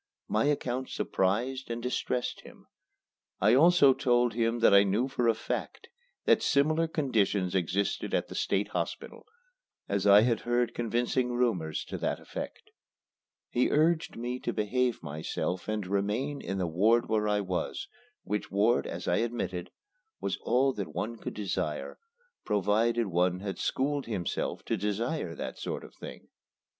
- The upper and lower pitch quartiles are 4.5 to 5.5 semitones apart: No, average, 4.1 semitones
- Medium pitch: No, low, 115 Hz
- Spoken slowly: No, average, 155 wpm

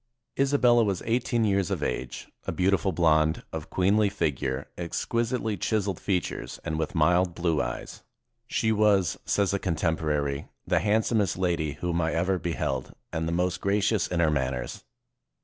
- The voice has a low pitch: Yes, very low, 90 Hz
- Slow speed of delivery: No, average, 155 wpm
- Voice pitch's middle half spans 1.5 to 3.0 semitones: No, average, 4.3 semitones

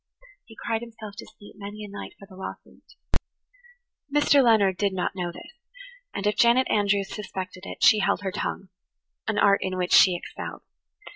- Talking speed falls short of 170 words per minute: No, average, 185 wpm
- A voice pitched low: No, high, 200 Hz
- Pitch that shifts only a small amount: No, average, 3.0 semitones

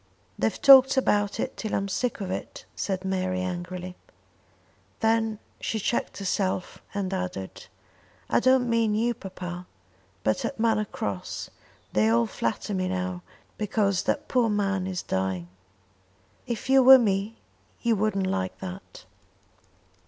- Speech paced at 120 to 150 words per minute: Yes, average, 140 wpm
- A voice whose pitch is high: Yes, high, 195 Hz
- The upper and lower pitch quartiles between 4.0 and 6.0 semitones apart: No, average, 3.5 semitones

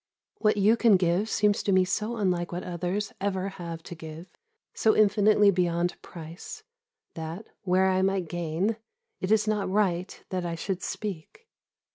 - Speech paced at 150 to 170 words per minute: Yes, average, 160 wpm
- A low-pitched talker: No, medium, 185 Hz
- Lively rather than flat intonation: No, average, 3.1 semitones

